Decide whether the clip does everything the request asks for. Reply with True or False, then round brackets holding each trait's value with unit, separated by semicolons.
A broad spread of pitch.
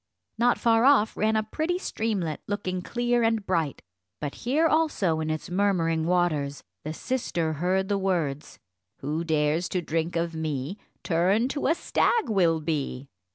True (5.8 semitones)